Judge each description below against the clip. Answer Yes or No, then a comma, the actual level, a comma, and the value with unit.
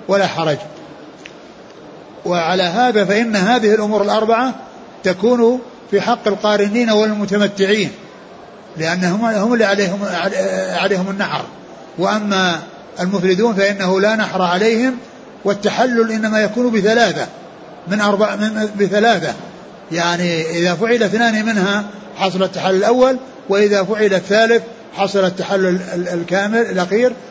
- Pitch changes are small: No, average, 3.2 semitones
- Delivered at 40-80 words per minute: No, average, 105 wpm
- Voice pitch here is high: Yes, high, 205 Hz